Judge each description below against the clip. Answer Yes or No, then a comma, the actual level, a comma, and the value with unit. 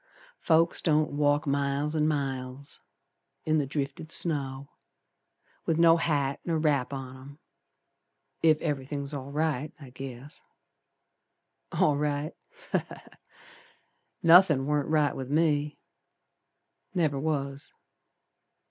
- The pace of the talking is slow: Yes, slow, 110 wpm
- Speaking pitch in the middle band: Yes, medium, 145 Hz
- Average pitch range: No, narrow, 2.1 semitones